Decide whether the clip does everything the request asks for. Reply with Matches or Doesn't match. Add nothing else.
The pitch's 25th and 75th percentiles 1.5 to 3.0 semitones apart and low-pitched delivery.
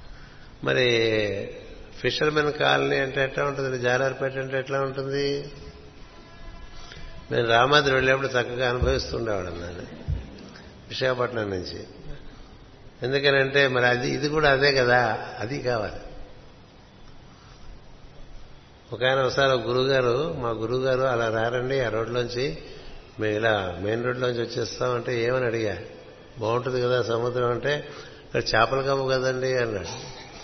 Matches